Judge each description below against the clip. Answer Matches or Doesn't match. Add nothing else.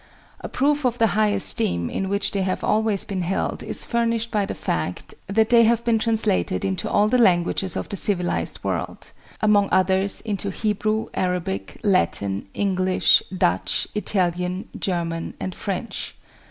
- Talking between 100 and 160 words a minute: Matches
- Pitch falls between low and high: Doesn't match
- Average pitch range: Matches